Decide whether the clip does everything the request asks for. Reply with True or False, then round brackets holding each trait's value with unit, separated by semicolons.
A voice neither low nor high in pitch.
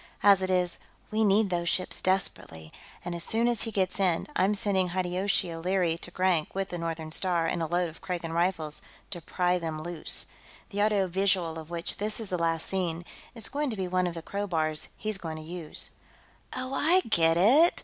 True (180 Hz)